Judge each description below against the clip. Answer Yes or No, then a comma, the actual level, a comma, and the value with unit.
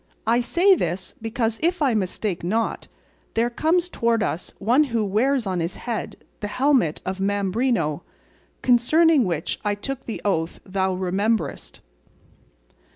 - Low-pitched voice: No, high, 225 Hz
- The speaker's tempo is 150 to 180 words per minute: No, average, 140 wpm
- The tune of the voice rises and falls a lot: No, average, 5.0 semitones